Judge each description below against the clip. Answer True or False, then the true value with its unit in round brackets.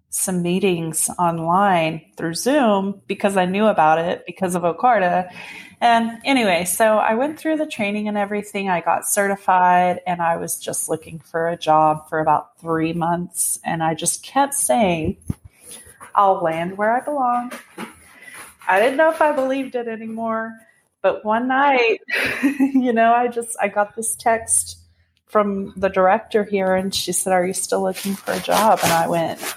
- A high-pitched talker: True (195 Hz)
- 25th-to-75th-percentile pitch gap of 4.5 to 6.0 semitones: True (5.0 semitones)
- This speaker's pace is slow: False (170 wpm)